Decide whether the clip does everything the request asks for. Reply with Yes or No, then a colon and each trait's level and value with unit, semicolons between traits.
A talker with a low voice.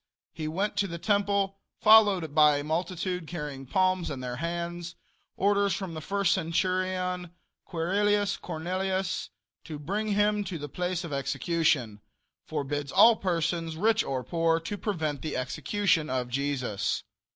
No: medium, 170 Hz